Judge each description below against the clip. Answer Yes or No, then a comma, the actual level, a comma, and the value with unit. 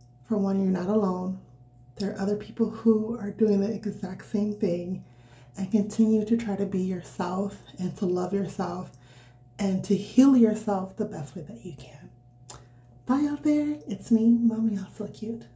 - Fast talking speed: No, average, 175 wpm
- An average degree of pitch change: Yes, average, 3.3 semitones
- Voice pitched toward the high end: Yes, high, 200 Hz